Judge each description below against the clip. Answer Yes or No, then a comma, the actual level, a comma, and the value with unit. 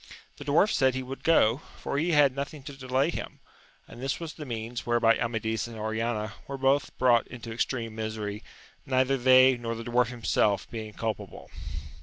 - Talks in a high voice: No, low, 120 Hz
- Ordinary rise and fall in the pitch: Yes, average, 3.2 semitones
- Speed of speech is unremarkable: Yes, average, 180 wpm